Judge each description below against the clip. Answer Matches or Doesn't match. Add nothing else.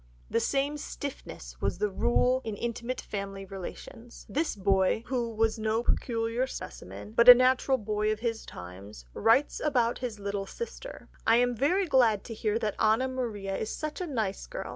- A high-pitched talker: Matches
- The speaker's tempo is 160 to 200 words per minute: Matches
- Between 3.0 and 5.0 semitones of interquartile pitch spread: Matches